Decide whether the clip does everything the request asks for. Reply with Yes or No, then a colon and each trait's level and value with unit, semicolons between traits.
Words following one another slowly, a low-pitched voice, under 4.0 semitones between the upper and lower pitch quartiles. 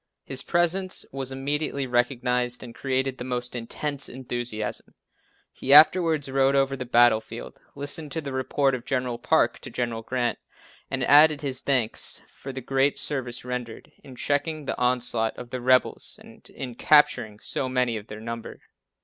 No: average, 160 wpm; low, 130 Hz; narrow, 2.4 semitones